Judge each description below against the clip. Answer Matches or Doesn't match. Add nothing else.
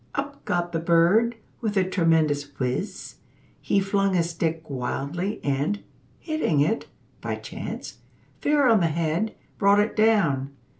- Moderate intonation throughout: Matches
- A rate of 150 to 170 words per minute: Doesn't match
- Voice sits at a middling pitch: Matches